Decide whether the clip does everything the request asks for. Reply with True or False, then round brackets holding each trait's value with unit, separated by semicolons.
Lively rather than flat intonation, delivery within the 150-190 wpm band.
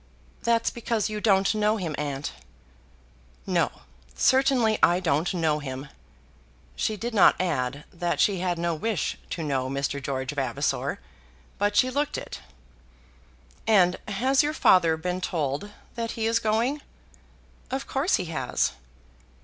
False (6.8 semitones; 140 wpm)